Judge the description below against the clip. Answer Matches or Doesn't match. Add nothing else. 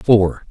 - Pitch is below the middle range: Matches